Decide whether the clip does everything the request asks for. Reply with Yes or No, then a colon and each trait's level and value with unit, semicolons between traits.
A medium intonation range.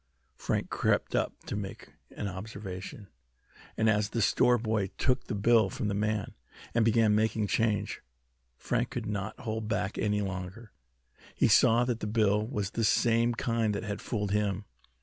No: narrow, 2.0 semitones